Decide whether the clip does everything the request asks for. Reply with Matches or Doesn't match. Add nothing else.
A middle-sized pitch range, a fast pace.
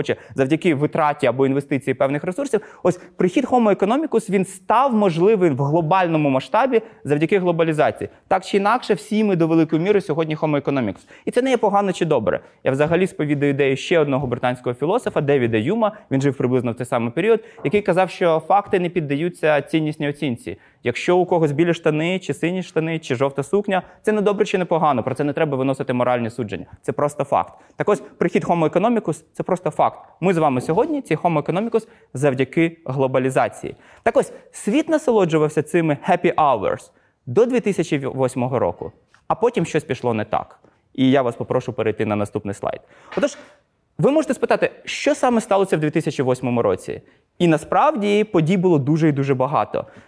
Doesn't match